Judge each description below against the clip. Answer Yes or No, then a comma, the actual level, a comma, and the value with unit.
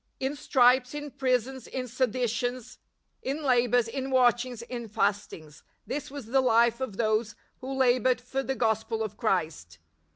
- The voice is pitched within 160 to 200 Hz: No, high, 245 Hz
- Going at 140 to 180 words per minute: Yes, average, 155 wpm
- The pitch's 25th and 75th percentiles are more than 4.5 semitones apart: No, average, 2.7 semitones